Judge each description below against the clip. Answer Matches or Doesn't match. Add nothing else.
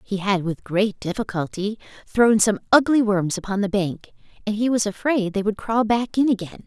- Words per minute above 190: Matches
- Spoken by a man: Doesn't match